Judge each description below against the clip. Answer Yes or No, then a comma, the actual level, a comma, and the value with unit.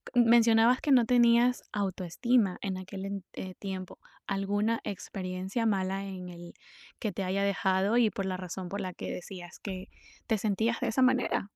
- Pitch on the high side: Yes, high, 200 Hz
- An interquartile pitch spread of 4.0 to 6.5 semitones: No, average, 3.4 semitones